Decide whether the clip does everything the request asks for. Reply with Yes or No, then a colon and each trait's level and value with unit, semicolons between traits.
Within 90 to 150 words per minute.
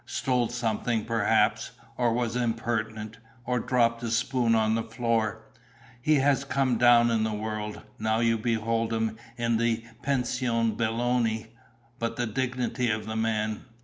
Yes: average, 145 wpm